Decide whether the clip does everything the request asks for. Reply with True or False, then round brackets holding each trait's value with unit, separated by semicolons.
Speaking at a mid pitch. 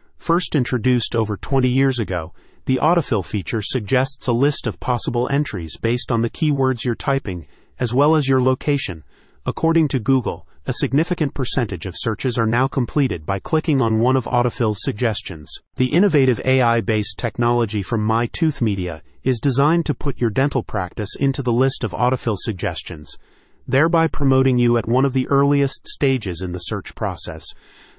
False (125 Hz)